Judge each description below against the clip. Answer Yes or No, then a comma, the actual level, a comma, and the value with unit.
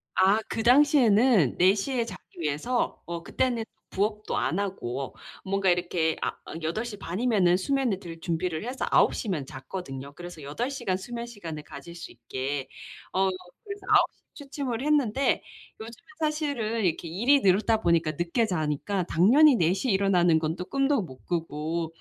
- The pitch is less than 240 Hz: Yes, high, 190 Hz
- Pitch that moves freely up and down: Yes, wide, 6.3 semitones